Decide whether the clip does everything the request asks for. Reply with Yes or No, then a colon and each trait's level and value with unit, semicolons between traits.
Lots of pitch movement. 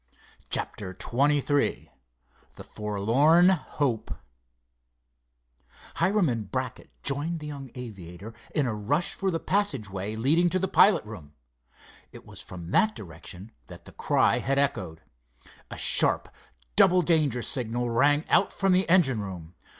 Yes: wide, 7.6 semitones